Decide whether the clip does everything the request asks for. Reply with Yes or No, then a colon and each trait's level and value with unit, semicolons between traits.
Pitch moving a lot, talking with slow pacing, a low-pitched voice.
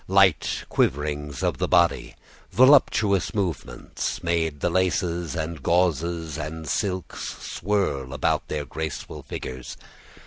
No: average, 3.7 semitones; slow, 110 wpm; very low, 85 Hz